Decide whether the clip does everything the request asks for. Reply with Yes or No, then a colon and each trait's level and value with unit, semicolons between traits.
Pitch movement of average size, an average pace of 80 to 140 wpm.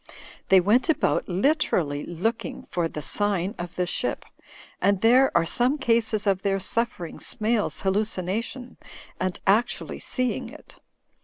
Yes: average, 4.5 semitones; slow, 135 wpm